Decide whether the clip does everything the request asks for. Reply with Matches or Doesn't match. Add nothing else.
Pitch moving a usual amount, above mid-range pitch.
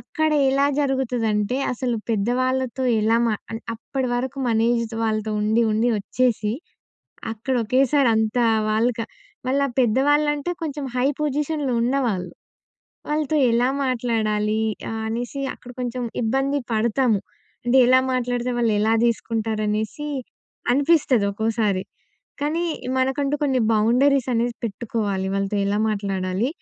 Matches